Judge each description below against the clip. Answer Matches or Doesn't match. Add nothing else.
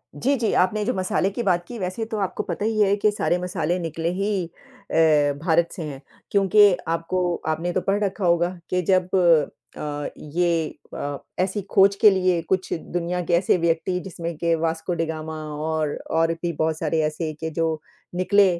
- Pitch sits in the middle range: Matches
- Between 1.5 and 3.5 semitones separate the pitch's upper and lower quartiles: Matches